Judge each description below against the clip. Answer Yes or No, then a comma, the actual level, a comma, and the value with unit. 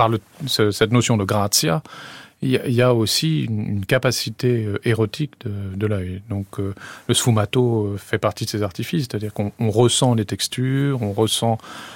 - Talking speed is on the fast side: No, average, 150 wpm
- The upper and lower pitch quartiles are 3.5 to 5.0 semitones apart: No, average, 3.1 semitones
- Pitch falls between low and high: No, low, 110 Hz